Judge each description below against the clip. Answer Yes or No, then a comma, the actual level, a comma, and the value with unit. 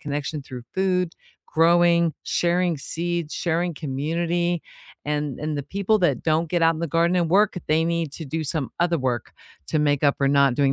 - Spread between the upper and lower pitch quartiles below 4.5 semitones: Yes, average, 2.9 semitones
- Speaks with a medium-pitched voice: Yes, medium, 165 Hz